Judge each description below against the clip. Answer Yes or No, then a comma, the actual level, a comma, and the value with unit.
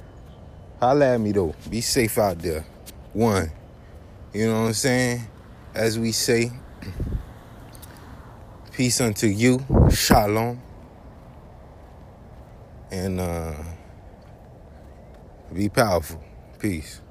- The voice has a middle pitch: No, low, 105 Hz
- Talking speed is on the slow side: Yes, slow, 90 wpm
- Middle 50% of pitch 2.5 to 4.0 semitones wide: No, average, 4.7 semitones